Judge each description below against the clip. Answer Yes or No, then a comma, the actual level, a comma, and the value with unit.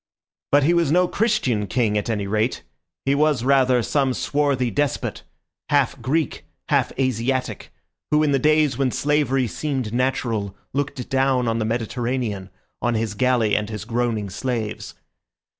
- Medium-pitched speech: No, low, 125 Hz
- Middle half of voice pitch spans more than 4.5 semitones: No, average, 3.8 semitones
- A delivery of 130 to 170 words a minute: Yes, average, 150 wpm